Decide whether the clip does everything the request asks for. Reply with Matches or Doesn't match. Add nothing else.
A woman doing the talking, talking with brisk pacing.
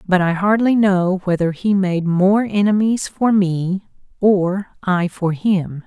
Doesn't match